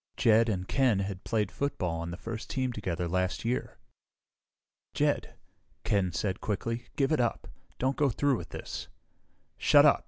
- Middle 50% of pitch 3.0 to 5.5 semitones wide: Yes, average, 5.1 semitones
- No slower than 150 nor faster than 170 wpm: Yes, average, 160 wpm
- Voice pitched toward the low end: Yes, low, 110 Hz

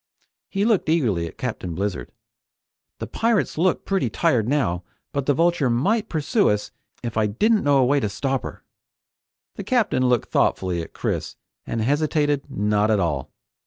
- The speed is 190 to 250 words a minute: No, average, 165 wpm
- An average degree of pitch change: No, wide, 8.1 semitones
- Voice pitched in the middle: No, low, 130 Hz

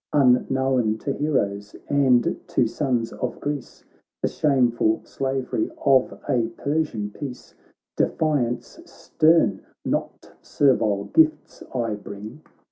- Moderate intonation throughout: Yes, average, 4.0 semitones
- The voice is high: No, low, 130 Hz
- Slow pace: Yes, slow, 105 wpm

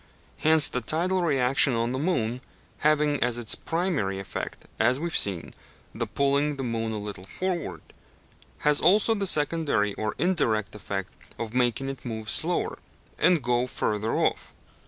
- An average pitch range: No, wide, 5.9 semitones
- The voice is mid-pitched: No, low, 125 Hz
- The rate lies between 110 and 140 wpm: No, average, 155 wpm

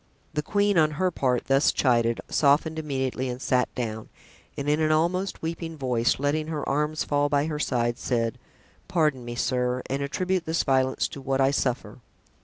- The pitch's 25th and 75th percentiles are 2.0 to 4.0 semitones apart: Yes, average, 3.6 semitones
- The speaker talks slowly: No, average, 180 wpm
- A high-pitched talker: No, medium, 140 Hz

